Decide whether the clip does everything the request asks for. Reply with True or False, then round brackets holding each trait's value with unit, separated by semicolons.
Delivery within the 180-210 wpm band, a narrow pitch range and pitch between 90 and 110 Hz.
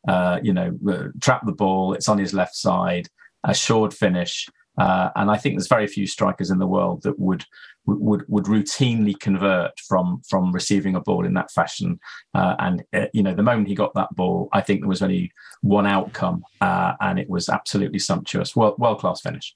True (205 wpm; 2.0 semitones; 100 Hz)